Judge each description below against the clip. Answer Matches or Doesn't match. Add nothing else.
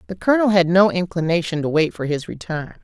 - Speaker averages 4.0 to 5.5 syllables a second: Doesn't match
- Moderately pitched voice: Matches